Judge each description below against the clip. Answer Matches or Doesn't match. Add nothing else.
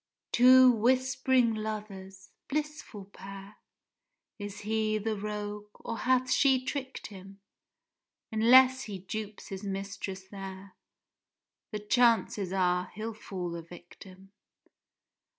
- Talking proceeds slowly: Matches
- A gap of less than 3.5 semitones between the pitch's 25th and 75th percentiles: Doesn't match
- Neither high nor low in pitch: Doesn't match